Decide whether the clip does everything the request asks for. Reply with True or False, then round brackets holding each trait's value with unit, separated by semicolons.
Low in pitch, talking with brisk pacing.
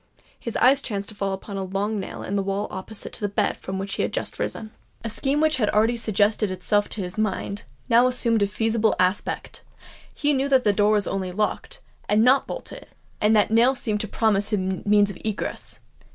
False (210 Hz; 210 wpm)